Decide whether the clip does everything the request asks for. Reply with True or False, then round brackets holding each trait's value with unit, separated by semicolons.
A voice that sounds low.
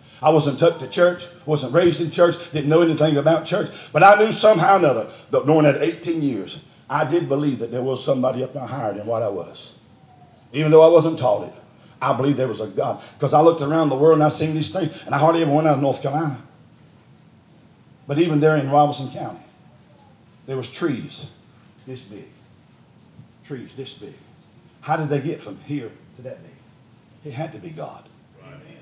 False (150 Hz)